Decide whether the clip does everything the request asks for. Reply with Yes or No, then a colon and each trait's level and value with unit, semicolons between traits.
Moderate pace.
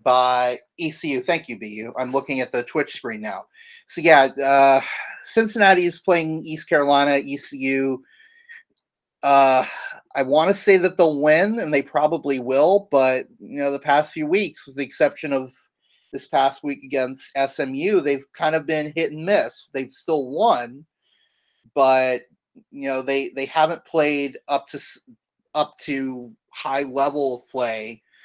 Yes: average, 155 wpm